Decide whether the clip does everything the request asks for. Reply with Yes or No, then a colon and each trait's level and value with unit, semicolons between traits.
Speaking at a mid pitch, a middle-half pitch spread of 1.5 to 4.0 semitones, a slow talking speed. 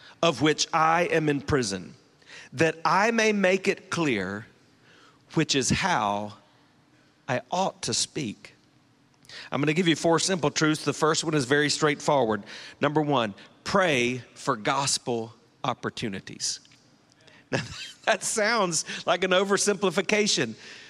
No: medium, 155 Hz; average, 4.8 semitones; slow, 125 wpm